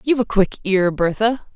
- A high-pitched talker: Yes, high, 210 Hz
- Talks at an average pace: Yes, average, 195 wpm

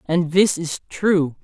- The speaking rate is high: No, average, 170 wpm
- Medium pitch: Yes, medium, 170 Hz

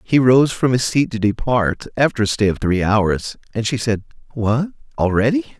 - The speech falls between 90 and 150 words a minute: No, average, 195 wpm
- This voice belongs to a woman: No, male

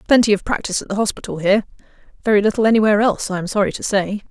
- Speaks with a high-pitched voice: Yes, high, 205 Hz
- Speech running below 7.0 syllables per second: No, 8.2 syllables/s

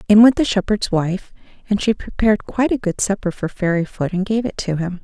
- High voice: Yes, high, 195 Hz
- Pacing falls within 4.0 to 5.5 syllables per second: No, 5.8 syllables/s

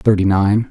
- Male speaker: Yes, male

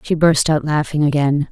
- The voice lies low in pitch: No, medium, 150 Hz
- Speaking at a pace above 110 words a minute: Yes, average, 200 wpm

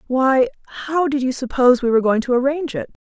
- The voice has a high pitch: Yes, very high, 260 Hz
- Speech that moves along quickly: Yes, fast, 220 wpm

